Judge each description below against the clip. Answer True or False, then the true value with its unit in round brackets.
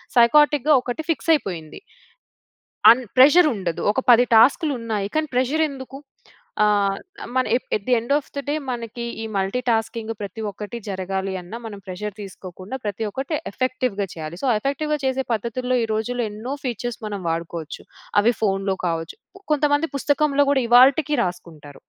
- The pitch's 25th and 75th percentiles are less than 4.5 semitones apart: False (5.2 semitones)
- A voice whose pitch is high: True (230 Hz)